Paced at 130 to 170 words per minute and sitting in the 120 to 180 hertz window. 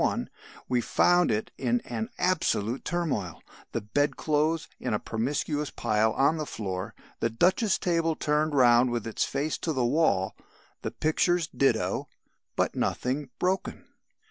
Yes: average, 145 wpm; medium, 140 Hz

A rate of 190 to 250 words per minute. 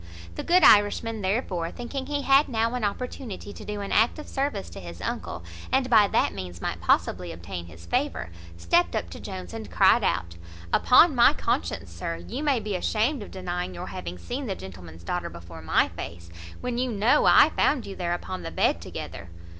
Yes: average, 200 wpm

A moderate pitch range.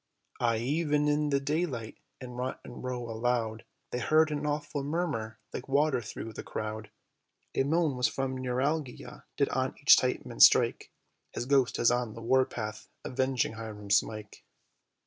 Yes: average, 4.2 semitones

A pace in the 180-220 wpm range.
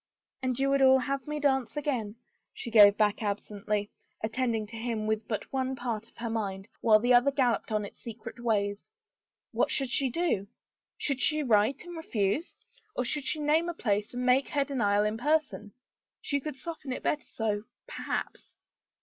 Yes: average, 190 wpm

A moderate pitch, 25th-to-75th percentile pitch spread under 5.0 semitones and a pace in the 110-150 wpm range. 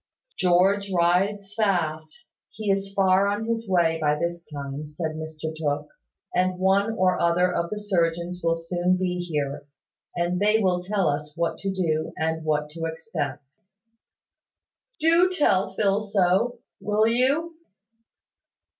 Yes: medium, 180 Hz; average, 3.8 semitones; average, 140 wpm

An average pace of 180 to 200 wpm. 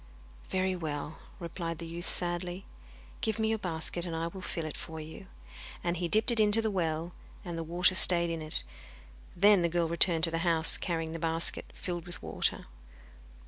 Yes: average, 190 wpm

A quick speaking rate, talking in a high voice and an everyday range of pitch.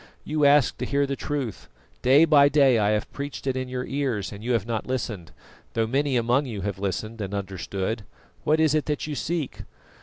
No: fast, 210 wpm; low, 125 Hz; average, 5.0 semitones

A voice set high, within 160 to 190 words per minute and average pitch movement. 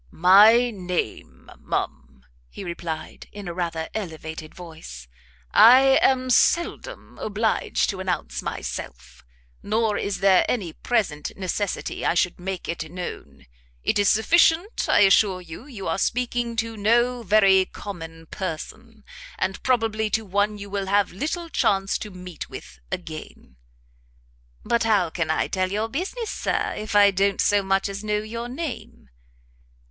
No: high, 200 Hz; average, 145 wpm; average, 3.9 semitones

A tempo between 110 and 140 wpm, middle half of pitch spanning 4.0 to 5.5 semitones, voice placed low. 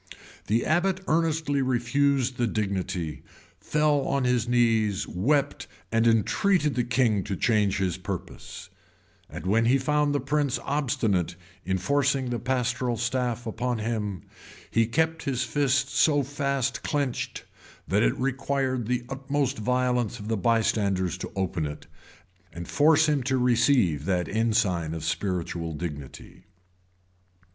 Yes: slow, 135 wpm; average, 5.2 semitones; low, 120 Hz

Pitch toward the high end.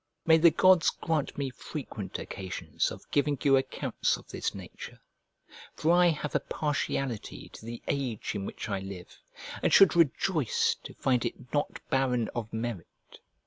No: low, 135 Hz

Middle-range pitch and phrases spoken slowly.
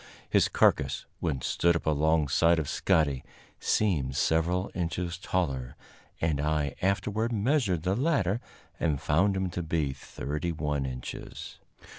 No: very low, 80 Hz; slow, 130 wpm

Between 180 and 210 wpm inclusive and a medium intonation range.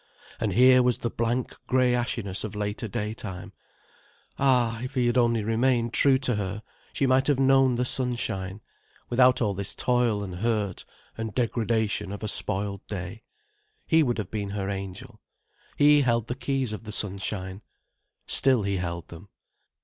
No: average, 165 wpm; average, 3.8 semitones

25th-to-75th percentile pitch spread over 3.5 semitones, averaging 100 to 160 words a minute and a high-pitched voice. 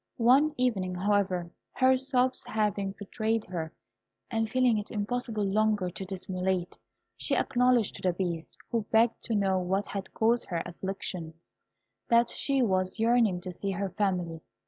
Yes: average, 4.0 semitones; average, 150 wpm; high, 205 Hz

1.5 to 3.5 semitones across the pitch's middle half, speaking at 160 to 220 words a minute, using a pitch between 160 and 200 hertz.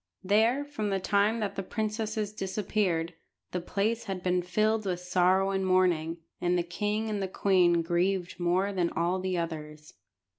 Yes: average, 2.9 semitones; average, 170 wpm; high, 190 Hz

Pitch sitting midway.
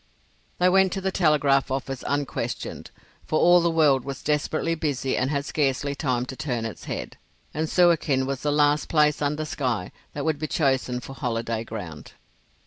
Yes: medium, 145 Hz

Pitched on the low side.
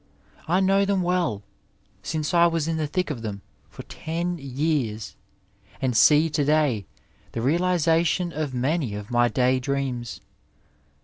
No: medium, 150 Hz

